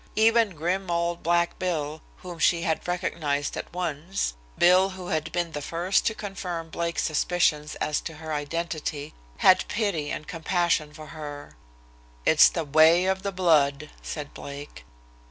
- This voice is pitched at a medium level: Yes, medium, 170 Hz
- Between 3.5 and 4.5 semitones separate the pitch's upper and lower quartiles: No, average, 2.9 semitones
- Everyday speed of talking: Yes, average, 155 wpm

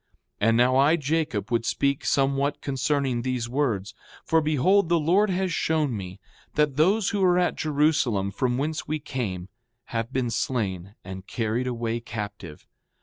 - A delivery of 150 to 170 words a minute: Yes, average, 160 wpm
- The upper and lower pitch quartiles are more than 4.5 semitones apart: Yes, average, 5.2 semitones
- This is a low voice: Yes, low, 130 Hz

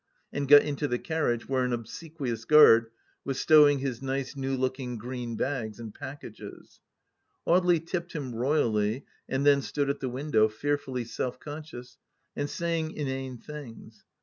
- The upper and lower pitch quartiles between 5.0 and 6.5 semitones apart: No, average, 3.2 semitones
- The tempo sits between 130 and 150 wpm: No, average, 165 wpm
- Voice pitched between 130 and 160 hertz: Yes, low, 135 Hz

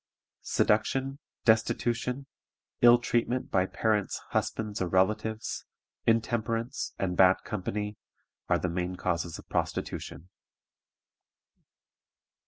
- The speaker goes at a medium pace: No, slow, 90 wpm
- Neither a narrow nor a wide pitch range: Yes, average, 4.0 semitones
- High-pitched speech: No, low, 110 Hz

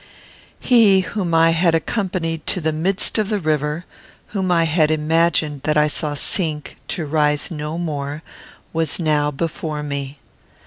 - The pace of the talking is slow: No, average, 150 wpm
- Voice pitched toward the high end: No, medium, 160 Hz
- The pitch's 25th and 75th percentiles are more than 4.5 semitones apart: No, narrow, 2.6 semitones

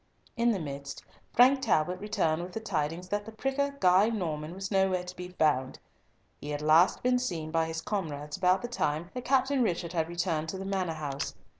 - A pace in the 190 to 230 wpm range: Yes, average, 200 wpm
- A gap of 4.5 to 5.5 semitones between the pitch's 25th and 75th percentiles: Yes, average, 4.9 semitones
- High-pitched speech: No, medium, 180 Hz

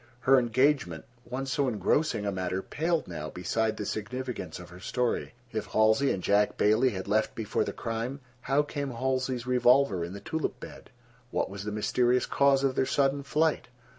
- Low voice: Yes, low, 120 Hz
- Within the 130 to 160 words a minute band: No, average, 180 wpm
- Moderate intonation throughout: Yes, average, 4.6 semitones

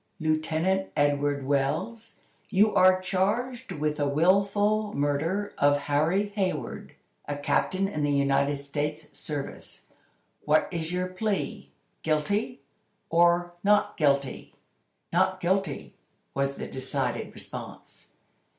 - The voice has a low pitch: No, medium, 160 Hz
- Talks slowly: Yes, slow, 110 wpm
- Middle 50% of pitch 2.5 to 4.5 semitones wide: No, average, 5.3 semitones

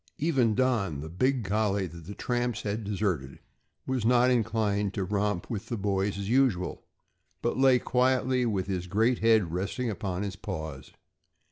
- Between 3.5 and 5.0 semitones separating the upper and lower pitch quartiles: Yes, average, 4.3 semitones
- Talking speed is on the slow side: No, average, 160 wpm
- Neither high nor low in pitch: No, low, 105 Hz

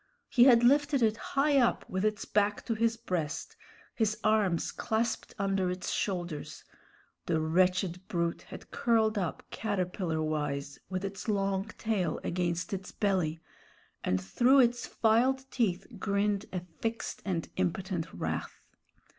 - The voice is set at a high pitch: Yes, high, 195 Hz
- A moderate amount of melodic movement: Yes, average, 4.2 semitones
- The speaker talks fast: No, average, 140 wpm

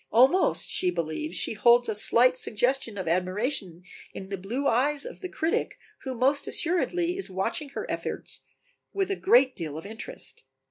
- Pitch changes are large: Yes, wide, 7.5 semitones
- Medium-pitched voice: No, high, 245 Hz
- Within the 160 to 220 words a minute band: Yes, average, 170 wpm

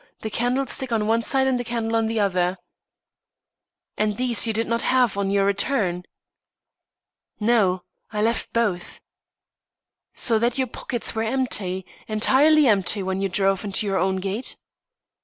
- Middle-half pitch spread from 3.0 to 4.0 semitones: Yes, average, 3.6 semitones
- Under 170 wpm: Yes, average, 155 wpm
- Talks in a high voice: Yes, high, 220 Hz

